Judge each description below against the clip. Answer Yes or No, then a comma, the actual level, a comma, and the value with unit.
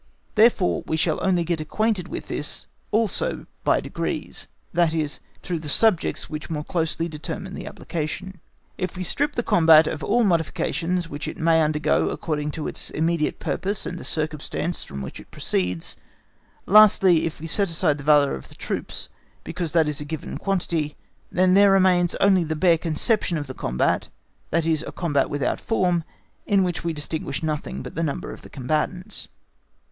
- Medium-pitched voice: Yes, medium, 165 Hz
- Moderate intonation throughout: Yes, average, 3.3 semitones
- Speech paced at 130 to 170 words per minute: No, average, 180 wpm